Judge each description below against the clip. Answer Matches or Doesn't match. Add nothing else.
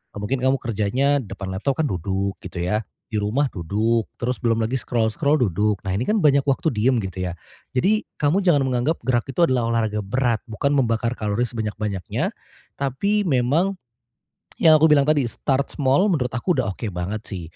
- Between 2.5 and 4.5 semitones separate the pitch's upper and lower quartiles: Doesn't match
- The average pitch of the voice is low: Matches